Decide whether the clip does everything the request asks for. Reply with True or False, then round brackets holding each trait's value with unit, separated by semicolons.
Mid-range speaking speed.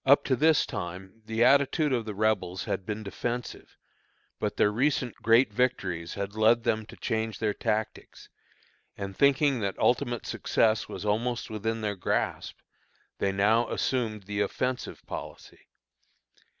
True (145 wpm)